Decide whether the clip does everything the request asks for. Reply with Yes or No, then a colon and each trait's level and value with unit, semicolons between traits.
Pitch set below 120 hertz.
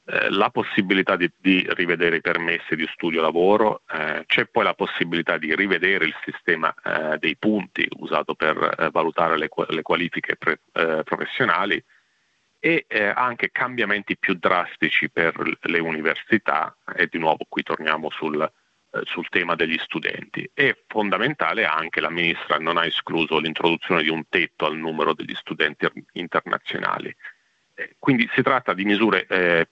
Yes: very low, 90 Hz